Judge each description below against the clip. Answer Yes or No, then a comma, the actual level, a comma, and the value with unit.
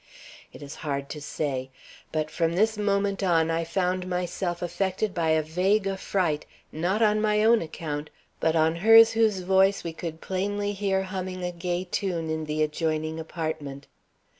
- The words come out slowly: No, average, 165 wpm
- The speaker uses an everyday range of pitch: Yes, average, 3.7 semitones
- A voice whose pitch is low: No, medium, 175 Hz